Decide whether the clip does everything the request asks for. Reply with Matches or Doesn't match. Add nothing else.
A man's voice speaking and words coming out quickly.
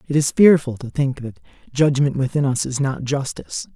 Doesn't match